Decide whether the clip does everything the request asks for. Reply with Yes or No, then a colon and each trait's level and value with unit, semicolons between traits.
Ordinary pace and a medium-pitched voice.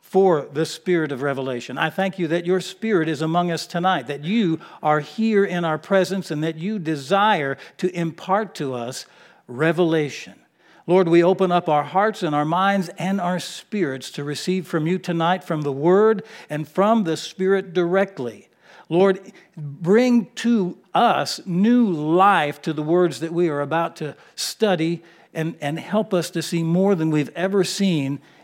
Yes: average, 175 wpm; medium, 175 Hz